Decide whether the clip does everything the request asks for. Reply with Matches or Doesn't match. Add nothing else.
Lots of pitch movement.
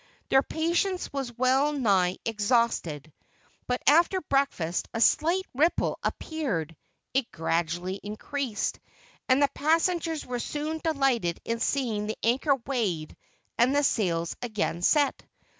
Matches